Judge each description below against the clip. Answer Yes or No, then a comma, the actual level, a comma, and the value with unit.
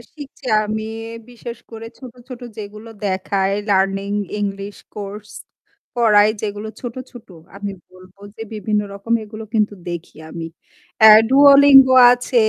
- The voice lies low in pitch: No, high, 210 Hz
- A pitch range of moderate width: Yes, average, 3.1 semitones